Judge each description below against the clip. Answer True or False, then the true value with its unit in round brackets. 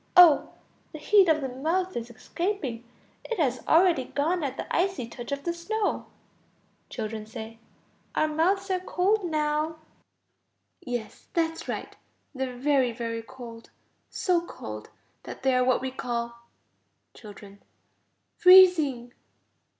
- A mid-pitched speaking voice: False (285 Hz)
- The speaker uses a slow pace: True (130 wpm)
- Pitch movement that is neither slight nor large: False (6.4 semitones)